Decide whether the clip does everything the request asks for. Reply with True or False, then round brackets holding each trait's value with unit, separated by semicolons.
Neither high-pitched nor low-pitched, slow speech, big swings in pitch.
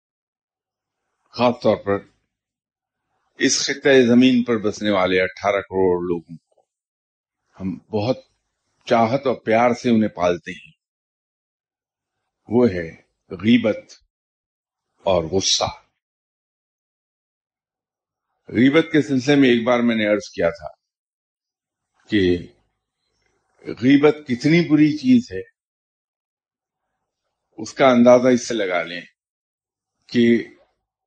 False (115 Hz; 100 wpm; 6.1 semitones)